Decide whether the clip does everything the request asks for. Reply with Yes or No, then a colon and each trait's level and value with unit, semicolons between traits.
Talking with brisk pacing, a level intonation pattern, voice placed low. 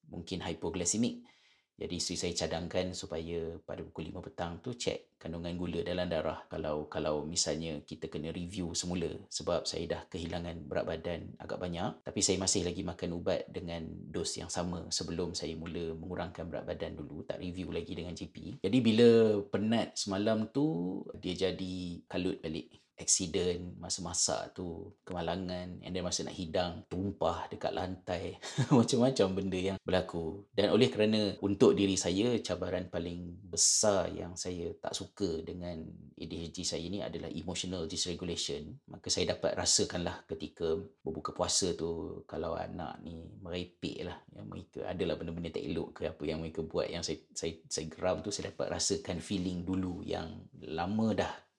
Yes: fast, 160 wpm; narrow, 2.2 semitones; very low, 90 Hz